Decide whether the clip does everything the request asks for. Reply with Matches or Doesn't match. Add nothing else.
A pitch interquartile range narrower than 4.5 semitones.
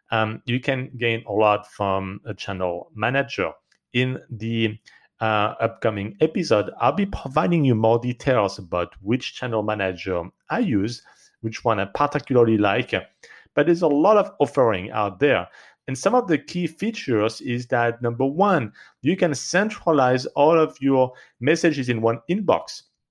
Doesn't match